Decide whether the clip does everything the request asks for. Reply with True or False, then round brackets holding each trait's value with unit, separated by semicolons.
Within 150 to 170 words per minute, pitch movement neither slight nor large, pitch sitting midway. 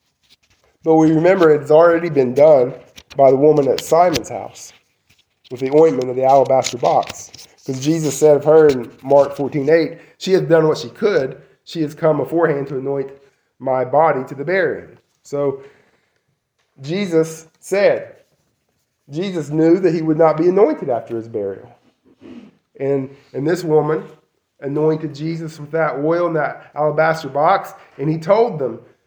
True (155 wpm; 3.1 semitones; 150 Hz)